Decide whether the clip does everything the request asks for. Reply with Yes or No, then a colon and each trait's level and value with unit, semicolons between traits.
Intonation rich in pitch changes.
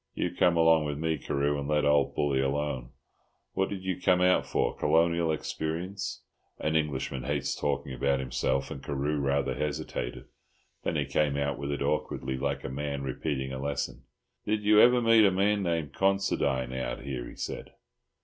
No: average, 3.8 semitones